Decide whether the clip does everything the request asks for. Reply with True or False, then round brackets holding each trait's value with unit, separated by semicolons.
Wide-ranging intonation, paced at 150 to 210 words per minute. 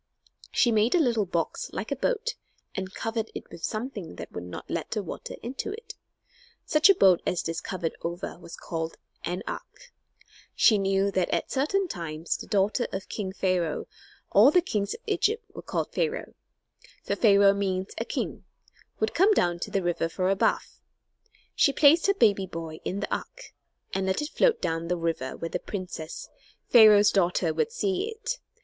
True (8.2 semitones; 185 wpm)